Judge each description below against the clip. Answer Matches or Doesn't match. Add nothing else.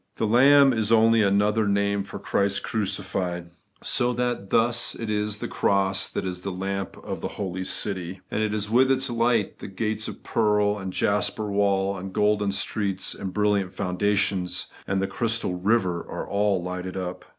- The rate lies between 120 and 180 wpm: Matches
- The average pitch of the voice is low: Matches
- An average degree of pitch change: Doesn't match